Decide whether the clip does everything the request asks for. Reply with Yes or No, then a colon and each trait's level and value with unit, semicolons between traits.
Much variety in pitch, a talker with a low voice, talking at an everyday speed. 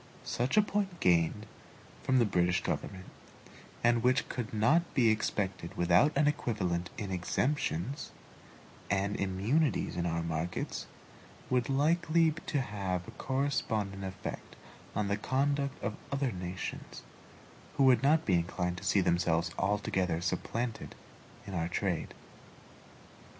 No: wide, 7.1 semitones; low, 105 Hz; slow, 130 wpm